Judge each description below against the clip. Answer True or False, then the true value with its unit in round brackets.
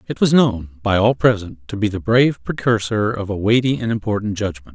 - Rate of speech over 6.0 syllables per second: False (5.5 syllables/s)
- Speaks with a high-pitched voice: False (105 Hz)